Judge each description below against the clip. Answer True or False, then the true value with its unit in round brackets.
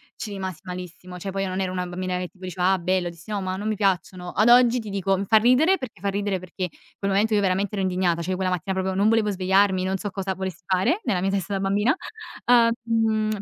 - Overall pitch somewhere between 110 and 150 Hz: False (190 Hz)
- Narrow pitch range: True (2.1 semitones)